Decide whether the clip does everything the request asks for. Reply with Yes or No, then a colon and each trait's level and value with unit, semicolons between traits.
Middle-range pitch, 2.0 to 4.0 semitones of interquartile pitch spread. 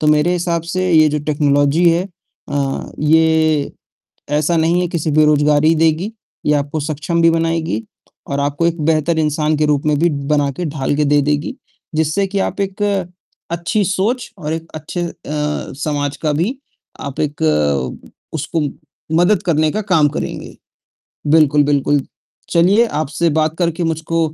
Yes: medium, 155 Hz; narrow, 2.4 semitones